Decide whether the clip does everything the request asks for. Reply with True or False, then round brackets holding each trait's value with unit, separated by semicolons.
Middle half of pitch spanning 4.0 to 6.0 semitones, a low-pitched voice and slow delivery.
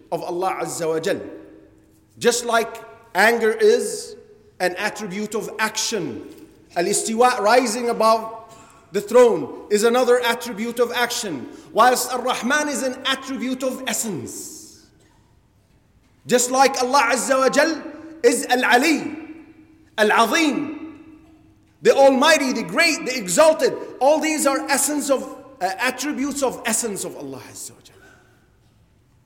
False (5.4 semitones; 240 Hz; 130 wpm)